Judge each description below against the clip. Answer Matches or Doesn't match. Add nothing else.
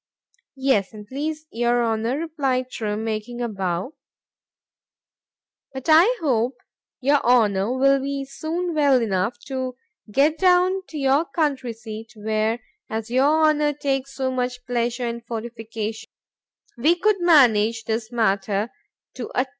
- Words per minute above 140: Doesn't match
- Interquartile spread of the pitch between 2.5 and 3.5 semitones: Doesn't match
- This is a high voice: Matches